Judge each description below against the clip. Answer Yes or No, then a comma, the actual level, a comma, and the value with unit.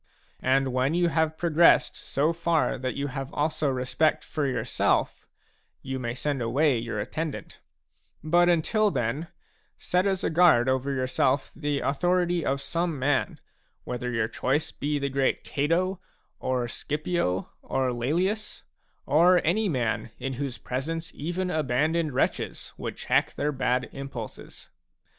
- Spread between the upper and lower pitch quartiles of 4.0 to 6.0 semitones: Yes, average, 4.4 semitones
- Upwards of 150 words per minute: No, average, 140 wpm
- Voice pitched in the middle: Yes, medium, 145 Hz